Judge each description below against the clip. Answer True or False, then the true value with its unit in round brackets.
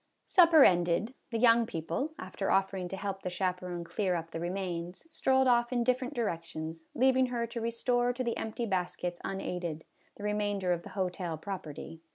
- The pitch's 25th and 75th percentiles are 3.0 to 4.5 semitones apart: False (5.2 semitones)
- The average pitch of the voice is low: False (195 Hz)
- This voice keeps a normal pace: True (175 wpm)